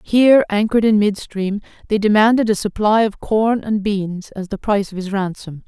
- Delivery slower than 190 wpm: No, average, 200 wpm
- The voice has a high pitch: Yes, high, 205 Hz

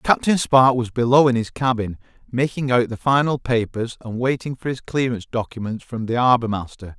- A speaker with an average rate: Yes, average, 190 wpm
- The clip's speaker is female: No, male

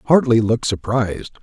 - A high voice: No, low, 115 Hz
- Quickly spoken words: No, slow, 125 wpm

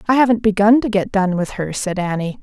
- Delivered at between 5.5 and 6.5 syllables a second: Yes, 5.8 syllables/s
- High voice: Yes, high, 205 Hz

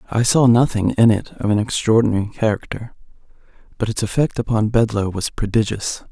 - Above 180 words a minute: No, average, 155 wpm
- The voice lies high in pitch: No, low, 110 Hz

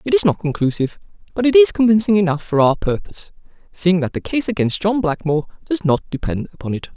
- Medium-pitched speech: Yes, medium, 180 Hz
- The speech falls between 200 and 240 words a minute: Yes, fast, 205 wpm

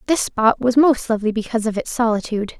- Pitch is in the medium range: No, high, 230 Hz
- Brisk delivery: Yes, fast, 210 wpm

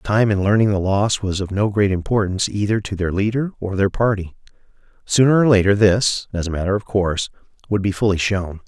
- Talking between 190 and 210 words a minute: Yes, fast, 205 wpm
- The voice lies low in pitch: Yes, low, 100 Hz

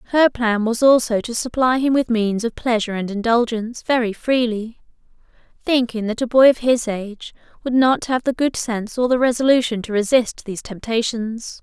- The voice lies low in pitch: No, high, 235 Hz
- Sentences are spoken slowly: No, average, 180 wpm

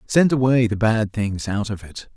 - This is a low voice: Yes, low, 110 Hz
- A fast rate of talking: Yes, fast, 220 wpm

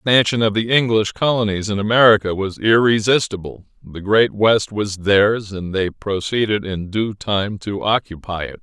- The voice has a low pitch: Yes, low, 105 Hz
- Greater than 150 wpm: Yes, average, 165 wpm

